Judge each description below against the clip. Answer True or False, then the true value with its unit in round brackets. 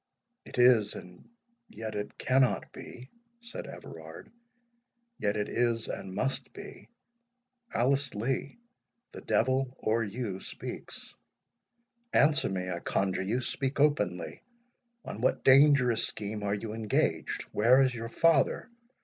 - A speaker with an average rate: False (115 wpm)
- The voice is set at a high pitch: False (120 Hz)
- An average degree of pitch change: True (4.5 semitones)